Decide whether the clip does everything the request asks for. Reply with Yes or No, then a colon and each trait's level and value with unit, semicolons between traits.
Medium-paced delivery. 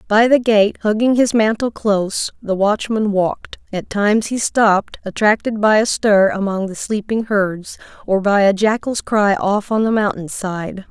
Yes: average, 175 wpm